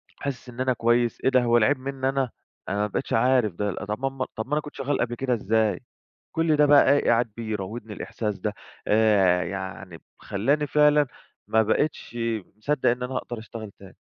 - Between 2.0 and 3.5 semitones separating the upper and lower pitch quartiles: No, average, 4.2 semitones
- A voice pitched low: Yes, low, 120 Hz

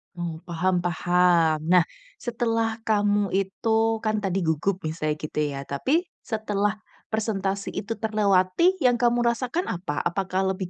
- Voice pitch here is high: Yes, high, 195 Hz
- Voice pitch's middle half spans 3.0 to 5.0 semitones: Yes, average, 4.2 semitones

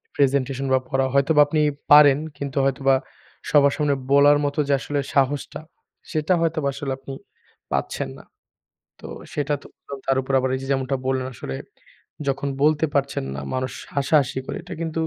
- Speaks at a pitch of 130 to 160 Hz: Yes, medium, 140 Hz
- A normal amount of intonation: No, narrow, 1.6 semitones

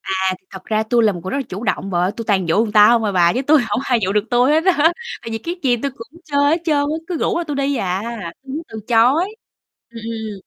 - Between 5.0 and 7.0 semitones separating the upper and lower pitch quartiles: Yes, wide, 5.6 semitones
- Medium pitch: No, high, 235 Hz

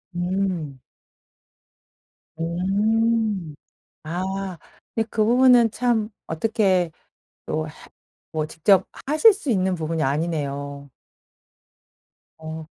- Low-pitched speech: No, medium, 185 Hz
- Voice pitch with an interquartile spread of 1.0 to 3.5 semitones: No, wide, 5.6 semitones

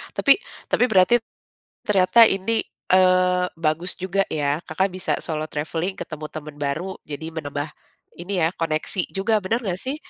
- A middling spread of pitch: Yes, average, 3.7 semitones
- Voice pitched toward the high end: No, medium, 180 Hz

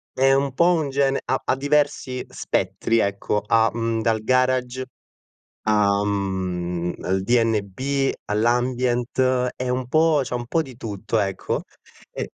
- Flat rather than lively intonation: No, average, 4.0 semitones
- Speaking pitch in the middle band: No, low, 120 Hz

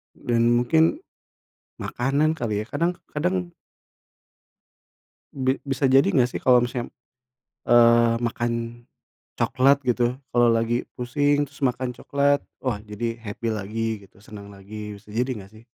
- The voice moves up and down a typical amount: Yes, average, 3.6 semitones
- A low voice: Yes, low, 120 Hz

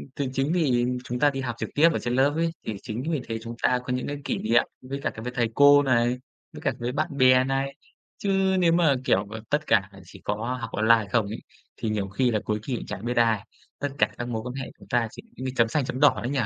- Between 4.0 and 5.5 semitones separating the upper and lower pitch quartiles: No, average, 3.6 semitones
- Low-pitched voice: Yes, low, 125 Hz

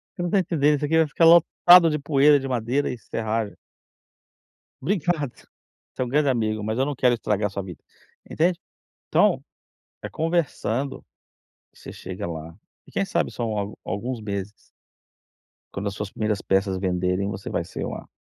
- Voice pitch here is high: No, low, 120 Hz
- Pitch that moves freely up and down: Yes, wide, 6.7 semitones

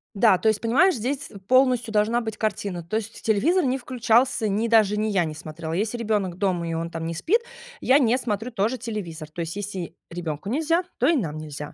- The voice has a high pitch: Yes, high, 215 Hz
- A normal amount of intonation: No, wide, 5.8 semitones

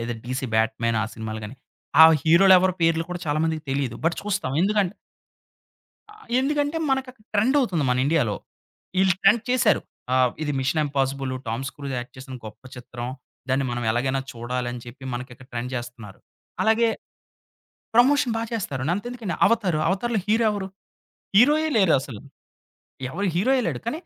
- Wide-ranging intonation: Yes, wide, 9.0 semitones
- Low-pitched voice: No, medium, 155 Hz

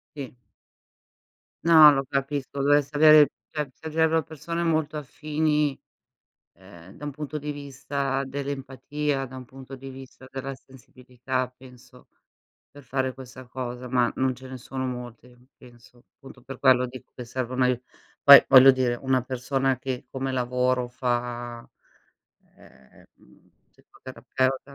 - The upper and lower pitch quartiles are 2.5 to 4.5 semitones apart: No, narrow, 2.1 semitones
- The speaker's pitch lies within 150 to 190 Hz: No, low, 130 Hz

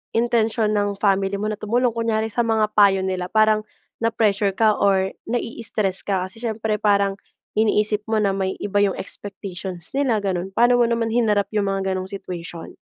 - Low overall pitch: No, high, 210 Hz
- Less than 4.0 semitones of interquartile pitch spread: Yes, narrow, 2.4 semitones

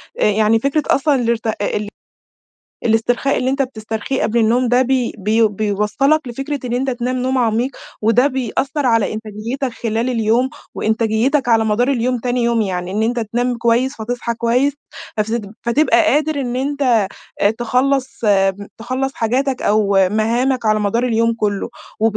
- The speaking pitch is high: Yes, high, 235 Hz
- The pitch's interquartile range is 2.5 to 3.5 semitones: Yes, average, 2.9 semitones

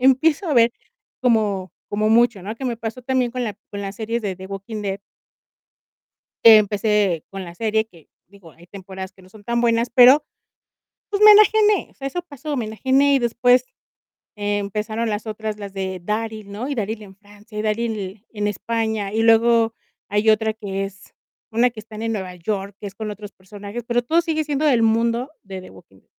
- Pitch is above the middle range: Yes, high, 220 Hz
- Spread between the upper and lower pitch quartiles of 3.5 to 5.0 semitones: No, average, 3.0 semitones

